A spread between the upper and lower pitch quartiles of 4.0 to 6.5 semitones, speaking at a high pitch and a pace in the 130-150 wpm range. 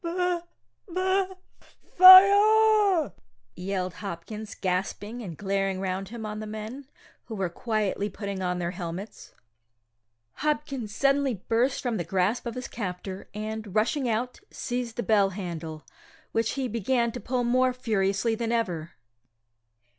Yes: average, 4.7 semitones; high, 220 Hz; slow, 135 wpm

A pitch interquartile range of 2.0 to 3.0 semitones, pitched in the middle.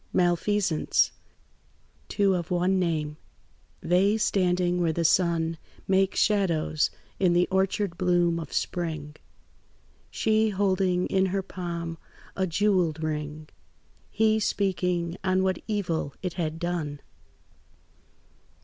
Yes: narrow, 2.5 semitones; medium, 180 Hz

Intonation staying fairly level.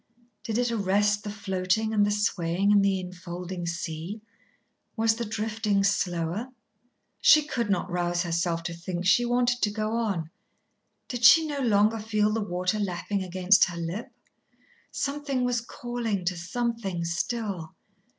No: average, 4.1 semitones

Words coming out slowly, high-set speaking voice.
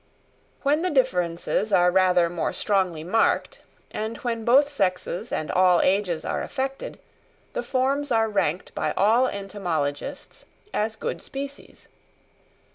Yes: slow, 125 wpm; high, 205 Hz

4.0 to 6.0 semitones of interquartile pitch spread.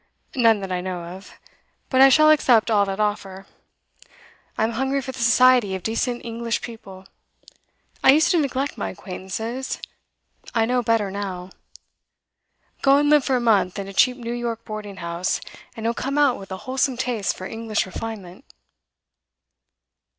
Yes: average, 4.7 semitones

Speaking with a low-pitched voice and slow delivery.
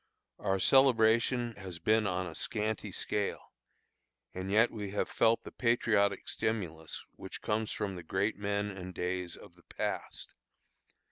No: low, 100 Hz; average, 145 wpm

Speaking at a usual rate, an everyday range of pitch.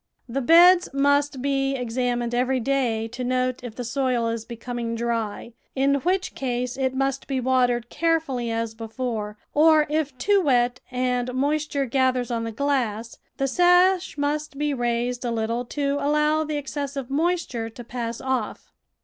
Yes: average, 160 wpm; average, 3.1 semitones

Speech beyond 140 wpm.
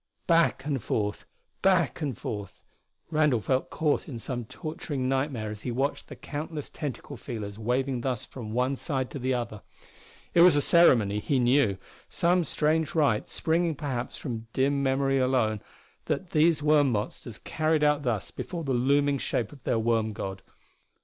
Yes: average, 165 wpm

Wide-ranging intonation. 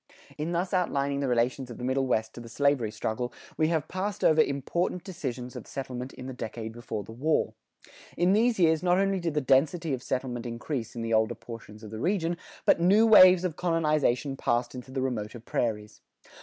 Yes: wide, 6.0 semitones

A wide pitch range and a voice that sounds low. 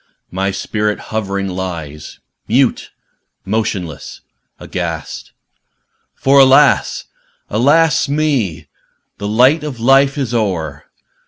Yes: wide, 6.1 semitones; low, 110 Hz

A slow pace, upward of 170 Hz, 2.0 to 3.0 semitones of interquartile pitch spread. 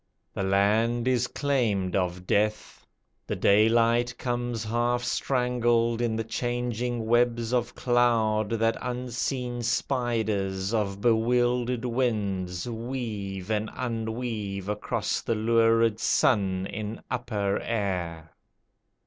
No: slow, 105 wpm; low, 115 Hz; average, 2.7 semitones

